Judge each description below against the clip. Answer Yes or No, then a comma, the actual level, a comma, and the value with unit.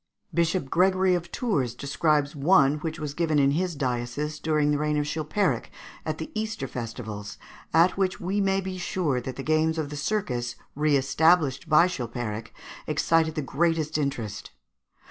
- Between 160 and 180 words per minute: Yes, average, 165 wpm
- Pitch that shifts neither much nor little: Yes, average, 4.0 semitones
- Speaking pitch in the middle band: Yes, medium, 150 Hz